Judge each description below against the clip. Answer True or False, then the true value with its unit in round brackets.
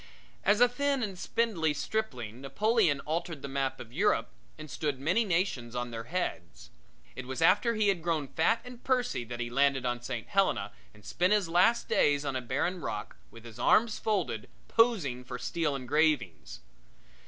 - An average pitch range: False (8.5 semitones)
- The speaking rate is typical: True (175 wpm)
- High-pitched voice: False (150 Hz)